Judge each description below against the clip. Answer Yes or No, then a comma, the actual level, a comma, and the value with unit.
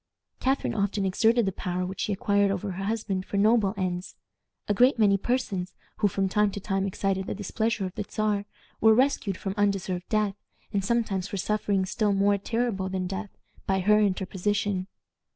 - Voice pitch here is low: No, high, 200 Hz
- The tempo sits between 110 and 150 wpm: No, average, 180 wpm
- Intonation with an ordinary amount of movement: No, narrow, 1.9 semitones